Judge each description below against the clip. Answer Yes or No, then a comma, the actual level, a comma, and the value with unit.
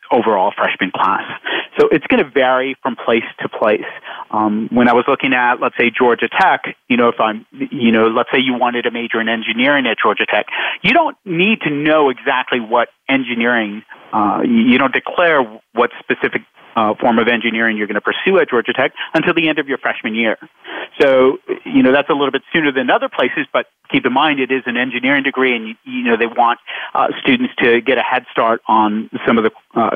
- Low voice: Yes, low, 130 Hz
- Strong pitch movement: Yes, wide, 5.8 semitones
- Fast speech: Yes, fast, 220 wpm